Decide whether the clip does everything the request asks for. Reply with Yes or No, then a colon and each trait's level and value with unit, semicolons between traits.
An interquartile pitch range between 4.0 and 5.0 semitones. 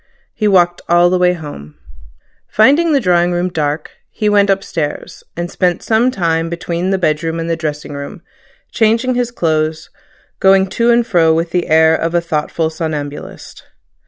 No: average, 3.4 semitones